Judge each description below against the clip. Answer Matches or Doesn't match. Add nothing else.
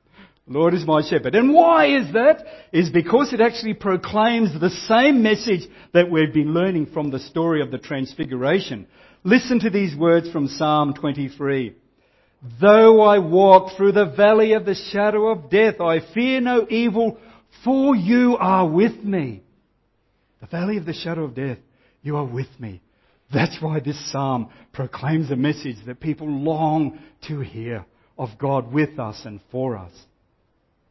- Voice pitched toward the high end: Doesn't match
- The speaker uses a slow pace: Doesn't match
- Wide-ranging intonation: Matches